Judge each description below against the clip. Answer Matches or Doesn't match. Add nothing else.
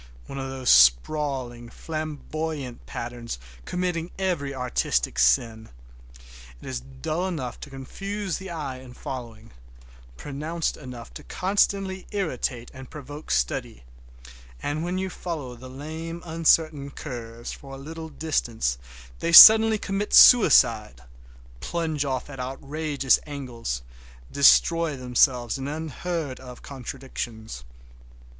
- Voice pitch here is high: Doesn't match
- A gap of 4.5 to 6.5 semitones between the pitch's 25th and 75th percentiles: Matches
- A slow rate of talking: Matches